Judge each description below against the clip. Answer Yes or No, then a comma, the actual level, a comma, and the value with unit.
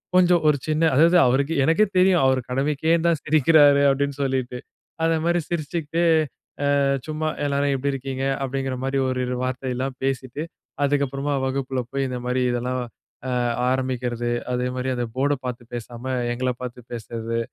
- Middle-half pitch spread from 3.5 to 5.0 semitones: No, average, 3.0 semitones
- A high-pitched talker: No, low, 135 Hz